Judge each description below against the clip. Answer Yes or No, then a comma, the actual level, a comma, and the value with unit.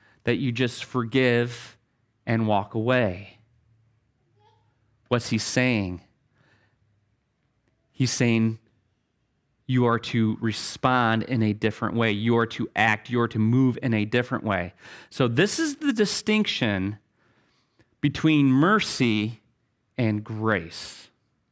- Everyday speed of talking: No, slow, 115 wpm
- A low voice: Yes, low, 115 Hz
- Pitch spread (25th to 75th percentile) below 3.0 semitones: Yes, narrow, 2.5 semitones